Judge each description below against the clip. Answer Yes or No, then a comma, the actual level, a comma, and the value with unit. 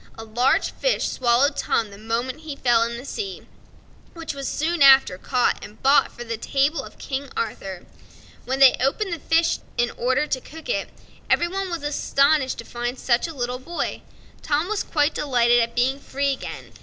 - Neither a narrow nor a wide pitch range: Yes, average, 4.2 semitones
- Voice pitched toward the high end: Yes, very high, 270 Hz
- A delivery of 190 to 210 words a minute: Yes, average, 195 wpm